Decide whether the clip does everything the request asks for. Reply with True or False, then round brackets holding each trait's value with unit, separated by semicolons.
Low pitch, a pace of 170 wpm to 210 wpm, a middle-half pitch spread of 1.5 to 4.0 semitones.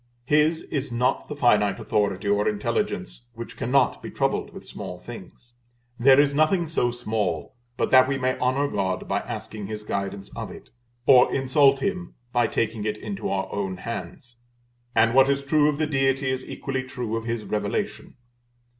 False (120 Hz; 175 wpm; 4.7 semitones)